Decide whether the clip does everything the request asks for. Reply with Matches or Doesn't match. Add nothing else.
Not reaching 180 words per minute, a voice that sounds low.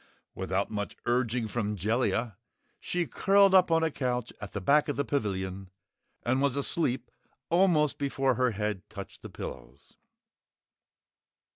Matches